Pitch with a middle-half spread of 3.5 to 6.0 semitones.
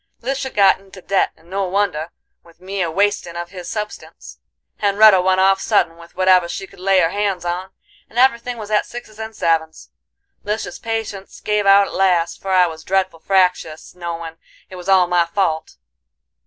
No: average, 2.9 semitones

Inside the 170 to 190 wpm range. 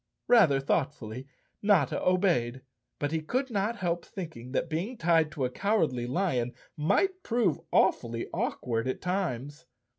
No: average, 140 wpm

